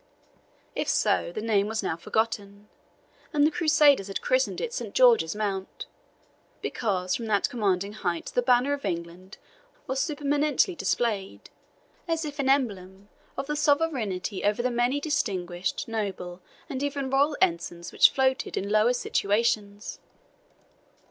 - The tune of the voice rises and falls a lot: Yes, wide, 6.5 semitones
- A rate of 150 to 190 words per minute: No, slow, 135 wpm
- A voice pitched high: Yes, high, 225 Hz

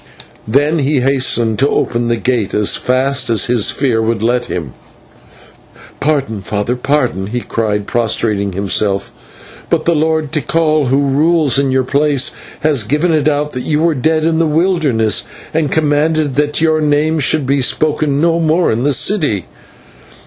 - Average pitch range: Yes, average, 4.7 semitones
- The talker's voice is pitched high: No, medium, 140 Hz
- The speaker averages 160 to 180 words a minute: Yes, average, 165 wpm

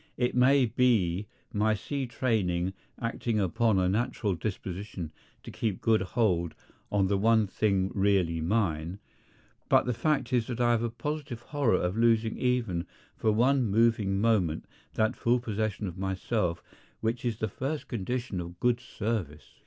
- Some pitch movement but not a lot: Yes, average, 4.0 semitones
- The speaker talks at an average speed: Yes, average, 155 wpm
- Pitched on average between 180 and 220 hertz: No, low, 110 Hz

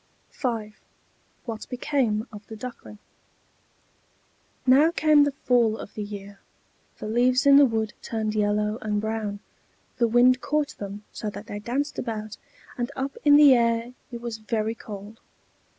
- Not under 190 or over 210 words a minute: No, average, 150 wpm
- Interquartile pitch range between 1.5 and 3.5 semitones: Yes, average, 3.2 semitones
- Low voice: No, high, 225 Hz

